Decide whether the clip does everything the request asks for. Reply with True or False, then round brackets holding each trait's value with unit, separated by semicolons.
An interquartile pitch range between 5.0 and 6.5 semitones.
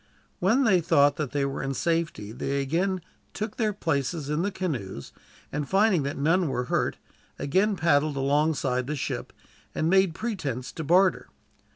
True (5.3 semitones)